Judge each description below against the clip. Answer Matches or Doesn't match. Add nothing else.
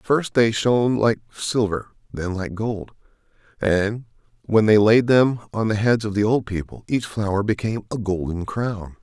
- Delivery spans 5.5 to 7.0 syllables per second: Doesn't match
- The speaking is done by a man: Matches